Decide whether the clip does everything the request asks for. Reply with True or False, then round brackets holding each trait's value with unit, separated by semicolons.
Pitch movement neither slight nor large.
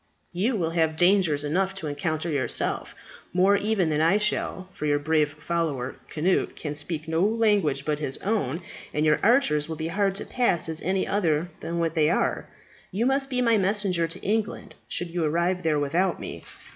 True (4.2 semitones)